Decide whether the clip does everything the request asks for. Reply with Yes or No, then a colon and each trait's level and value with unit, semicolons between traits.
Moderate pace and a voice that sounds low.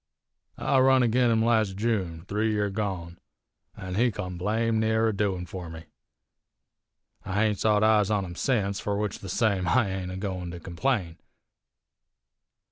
Yes: average, 165 wpm; low, 105 Hz